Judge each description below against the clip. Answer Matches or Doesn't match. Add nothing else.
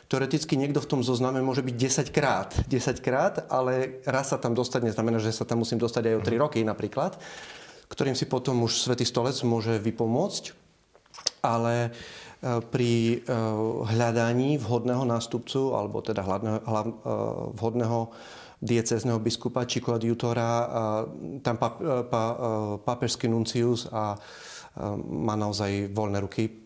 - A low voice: Matches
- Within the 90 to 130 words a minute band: Matches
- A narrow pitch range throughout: Matches